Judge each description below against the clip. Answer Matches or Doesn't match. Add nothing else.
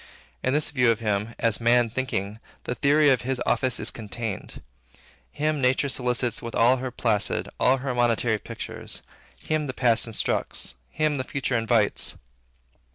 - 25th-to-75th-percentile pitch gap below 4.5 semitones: Matches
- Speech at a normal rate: Matches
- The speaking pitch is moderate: Doesn't match